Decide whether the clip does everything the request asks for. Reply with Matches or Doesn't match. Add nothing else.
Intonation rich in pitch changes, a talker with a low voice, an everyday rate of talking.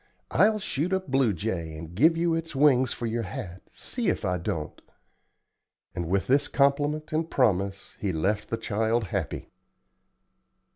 Matches